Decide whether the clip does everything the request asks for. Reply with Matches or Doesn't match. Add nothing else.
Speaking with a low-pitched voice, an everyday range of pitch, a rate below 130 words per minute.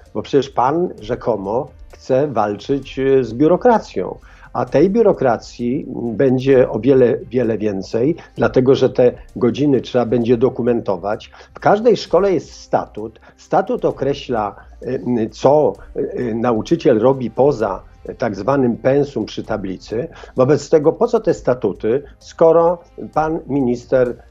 Matches